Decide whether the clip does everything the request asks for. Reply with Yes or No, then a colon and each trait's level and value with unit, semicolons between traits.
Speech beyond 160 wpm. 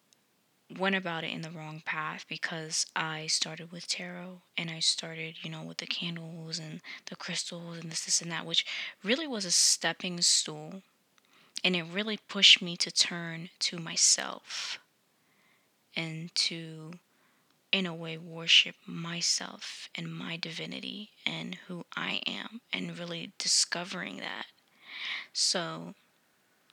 No: average, 140 wpm